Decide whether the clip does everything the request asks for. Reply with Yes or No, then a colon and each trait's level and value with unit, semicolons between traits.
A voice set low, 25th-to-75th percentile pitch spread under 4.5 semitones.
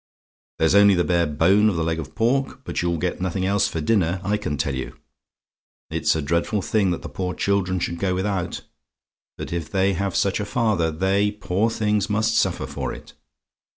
Yes: very low, 95 Hz; average, 3.4 semitones